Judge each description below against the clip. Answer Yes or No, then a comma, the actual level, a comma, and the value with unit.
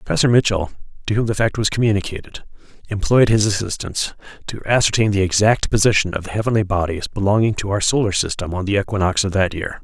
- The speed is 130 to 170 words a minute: No, average, 190 wpm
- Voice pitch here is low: Yes, low, 100 Hz